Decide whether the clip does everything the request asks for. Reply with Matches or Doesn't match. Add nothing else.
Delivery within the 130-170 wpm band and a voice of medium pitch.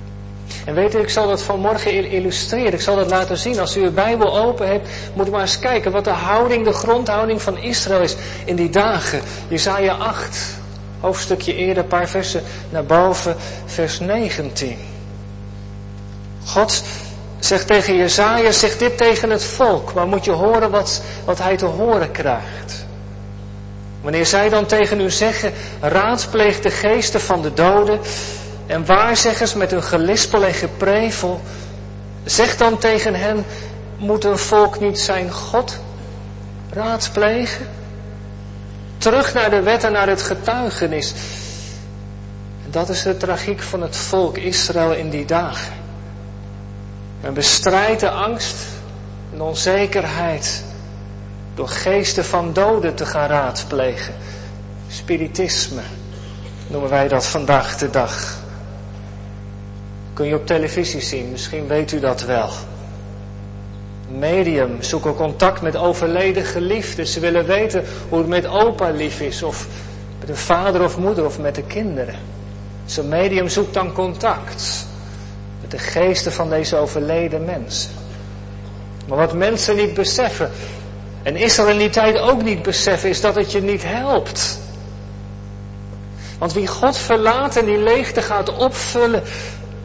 Matches